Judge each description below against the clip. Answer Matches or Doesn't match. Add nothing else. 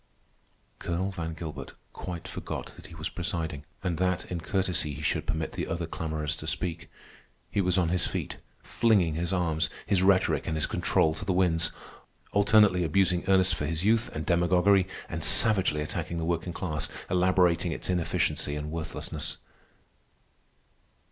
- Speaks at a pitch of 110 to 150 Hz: Doesn't match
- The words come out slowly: Doesn't match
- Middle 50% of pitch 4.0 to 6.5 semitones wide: Doesn't match